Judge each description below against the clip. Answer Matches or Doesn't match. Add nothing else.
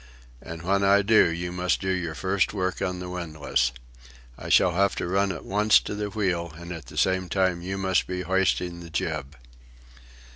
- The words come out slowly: Doesn't match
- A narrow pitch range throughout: Matches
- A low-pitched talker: Matches